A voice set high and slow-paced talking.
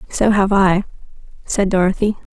Yes: high, 195 Hz; slow, 130 wpm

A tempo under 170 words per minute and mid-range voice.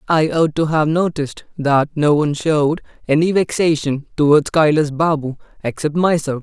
Yes: average, 150 wpm; medium, 155 Hz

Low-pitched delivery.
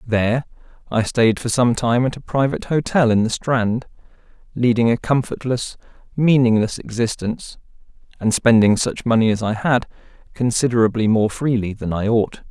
Yes: low, 115 Hz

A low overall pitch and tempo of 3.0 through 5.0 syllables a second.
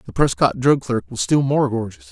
No: low, 130 Hz; 5.3 syllables/s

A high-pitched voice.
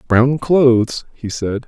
No: low, 125 Hz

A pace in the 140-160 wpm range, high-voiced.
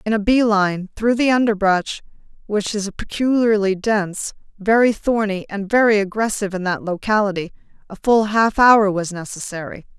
Yes: average, 150 wpm; high, 205 Hz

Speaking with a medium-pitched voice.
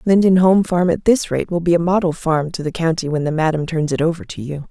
Yes: medium, 165 Hz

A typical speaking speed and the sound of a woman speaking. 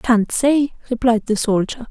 Yes: average, 160 wpm; female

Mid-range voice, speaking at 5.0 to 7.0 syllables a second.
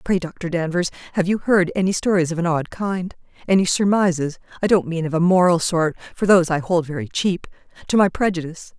Yes: medium, 175 Hz; 6.0 syllables/s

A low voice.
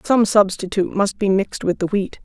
No: high, 200 Hz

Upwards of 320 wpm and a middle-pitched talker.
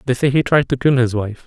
No: fast, 330 wpm; low, 130 Hz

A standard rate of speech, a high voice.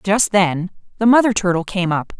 Yes: average, 190 wpm; high, 195 Hz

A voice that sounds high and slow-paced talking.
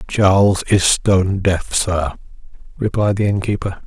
No: very low, 95 Hz; slow, 125 wpm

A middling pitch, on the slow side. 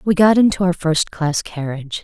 No: medium, 175 Hz; average, 175 wpm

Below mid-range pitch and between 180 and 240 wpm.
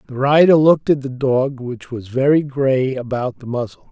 Yes: low, 130 Hz; average, 200 wpm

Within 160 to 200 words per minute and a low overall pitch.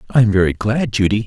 No: fast, 235 wpm; low, 105 Hz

